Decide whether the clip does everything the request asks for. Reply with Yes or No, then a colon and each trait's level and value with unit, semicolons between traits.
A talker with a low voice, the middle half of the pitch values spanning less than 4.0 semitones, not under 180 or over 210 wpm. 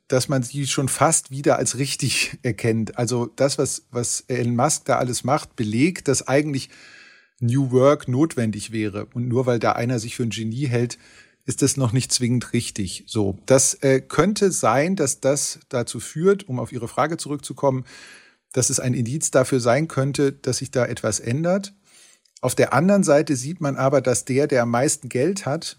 Yes: low, 130 Hz; average, 3.1 semitones; fast, 190 wpm